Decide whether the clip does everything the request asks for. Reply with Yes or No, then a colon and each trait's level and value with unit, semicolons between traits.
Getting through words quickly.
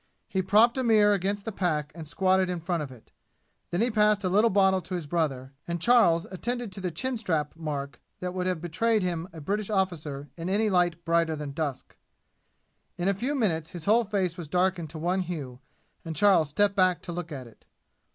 Yes: fast, 210 wpm